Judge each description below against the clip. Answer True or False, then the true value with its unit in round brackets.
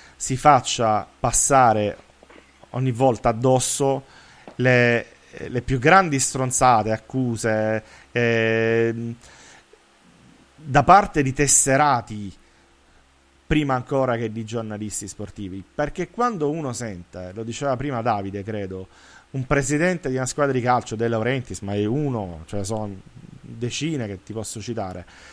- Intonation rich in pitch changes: False (4.3 semitones)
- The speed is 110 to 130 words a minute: True (120 wpm)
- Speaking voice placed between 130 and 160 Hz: False (115 Hz)